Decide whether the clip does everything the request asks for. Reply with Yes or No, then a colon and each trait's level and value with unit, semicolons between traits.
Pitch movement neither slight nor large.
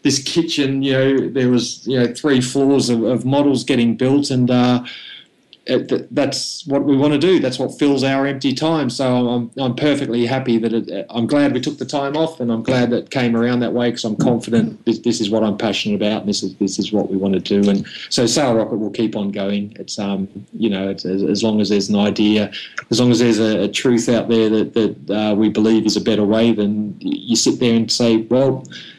Yes: average, 4.0 semitones